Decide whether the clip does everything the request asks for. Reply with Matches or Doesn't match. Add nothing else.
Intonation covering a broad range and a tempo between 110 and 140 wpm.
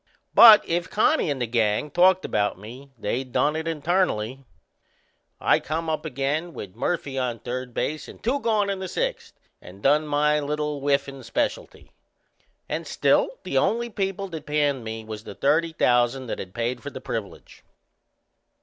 Doesn't match